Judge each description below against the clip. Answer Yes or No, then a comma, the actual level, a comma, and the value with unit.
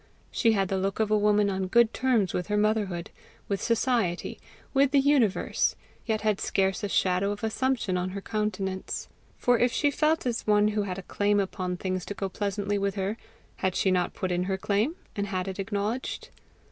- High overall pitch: Yes, high, 205 Hz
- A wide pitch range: No, narrow, 2.5 semitones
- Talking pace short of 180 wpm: No, average, 200 wpm